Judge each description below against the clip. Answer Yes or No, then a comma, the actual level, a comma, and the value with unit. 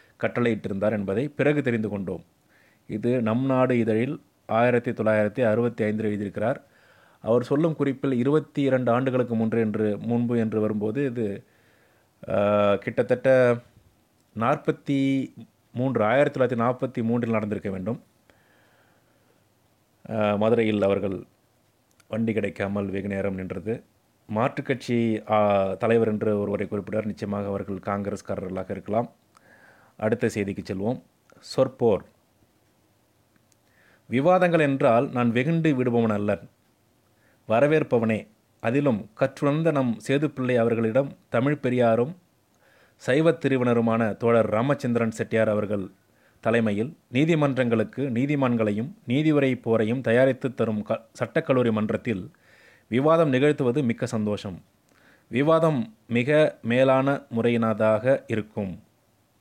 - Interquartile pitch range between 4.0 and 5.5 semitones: No, average, 3.4 semitones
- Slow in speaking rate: No, average, 95 wpm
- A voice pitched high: No, low, 115 Hz